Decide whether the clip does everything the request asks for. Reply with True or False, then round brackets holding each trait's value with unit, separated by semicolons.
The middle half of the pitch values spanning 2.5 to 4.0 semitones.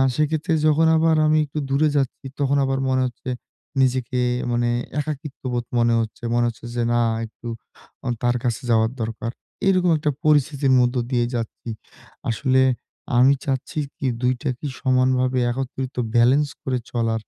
True (3.0 semitones)